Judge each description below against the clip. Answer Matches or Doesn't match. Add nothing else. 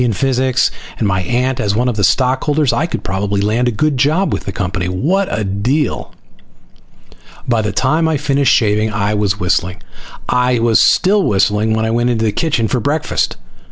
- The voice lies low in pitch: Matches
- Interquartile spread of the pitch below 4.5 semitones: Doesn't match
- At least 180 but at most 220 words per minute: Matches